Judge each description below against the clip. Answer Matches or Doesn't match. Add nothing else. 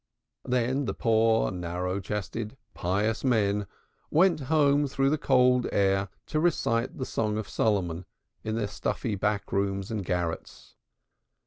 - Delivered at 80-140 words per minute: Matches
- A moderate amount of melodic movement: Matches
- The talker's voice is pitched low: Matches